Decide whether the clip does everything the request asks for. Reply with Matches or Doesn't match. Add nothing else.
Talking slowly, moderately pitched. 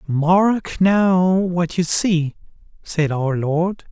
Matches